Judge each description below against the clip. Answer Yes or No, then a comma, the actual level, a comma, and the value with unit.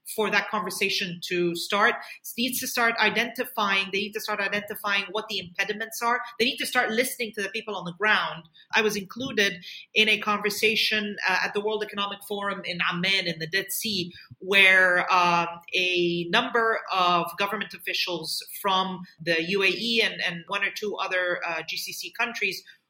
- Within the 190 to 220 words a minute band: No, average, 175 wpm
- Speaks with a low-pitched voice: No, high, 200 Hz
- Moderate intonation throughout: Yes, average, 3.1 semitones